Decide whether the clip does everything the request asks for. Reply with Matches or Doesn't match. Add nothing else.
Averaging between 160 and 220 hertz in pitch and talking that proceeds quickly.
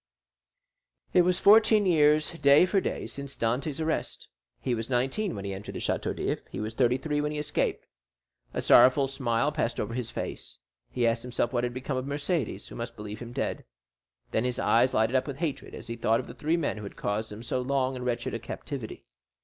Doesn't match